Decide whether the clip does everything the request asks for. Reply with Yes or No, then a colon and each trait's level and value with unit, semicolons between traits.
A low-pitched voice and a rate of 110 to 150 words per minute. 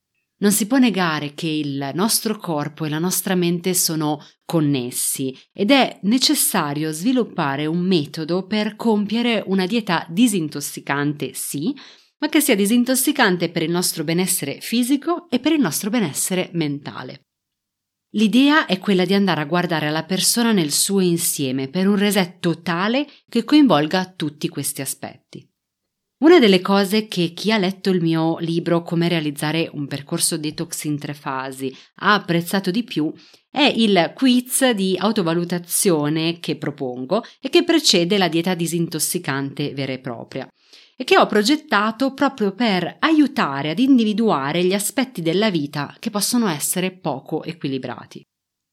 No: medium, 180 Hz; average, 145 wpm